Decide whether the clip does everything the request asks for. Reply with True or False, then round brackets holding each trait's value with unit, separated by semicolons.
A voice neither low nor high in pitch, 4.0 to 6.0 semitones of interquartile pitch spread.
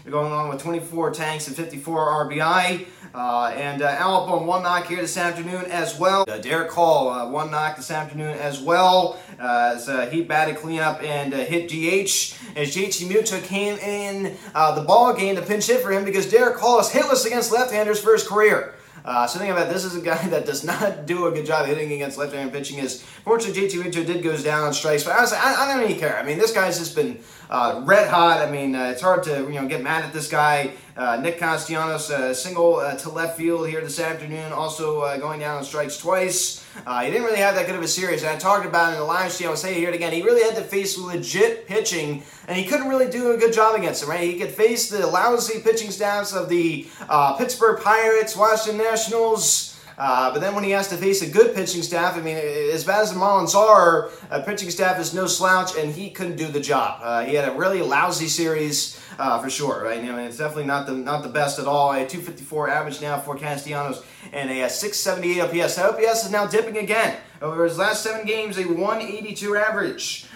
True (170 Hz; 5.0 semitones)